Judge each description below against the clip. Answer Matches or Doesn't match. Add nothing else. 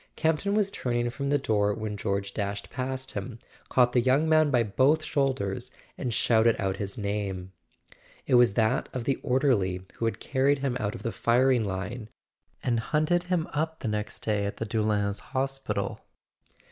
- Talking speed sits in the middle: Matches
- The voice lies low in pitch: Matches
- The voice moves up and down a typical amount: Matches